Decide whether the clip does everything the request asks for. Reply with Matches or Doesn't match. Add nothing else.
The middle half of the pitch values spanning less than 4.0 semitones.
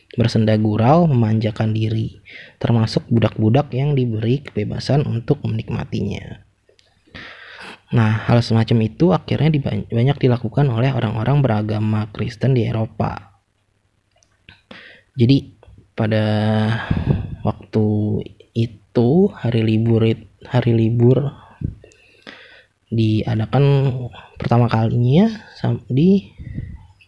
Matches